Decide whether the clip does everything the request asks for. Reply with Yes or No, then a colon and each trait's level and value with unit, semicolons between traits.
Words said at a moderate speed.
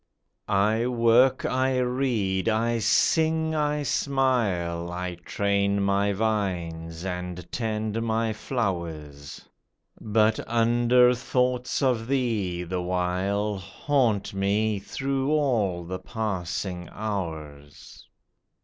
No: slow, 95 wpm